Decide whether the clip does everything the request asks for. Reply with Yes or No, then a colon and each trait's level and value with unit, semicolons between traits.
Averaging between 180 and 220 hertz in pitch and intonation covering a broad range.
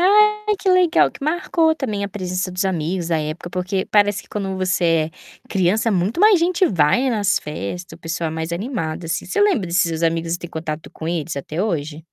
Yes: medium, 185 Hz; wide, 6.3 semitones